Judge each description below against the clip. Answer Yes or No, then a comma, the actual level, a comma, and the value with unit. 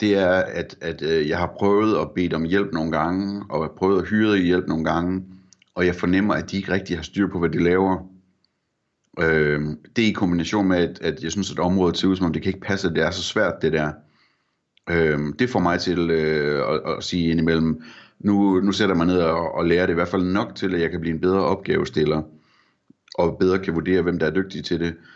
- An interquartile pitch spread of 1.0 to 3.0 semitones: Yes, average, 2.7 semitones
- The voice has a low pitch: Yes, very low, 90 Hz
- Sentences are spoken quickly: Yes, fast, 245 wpm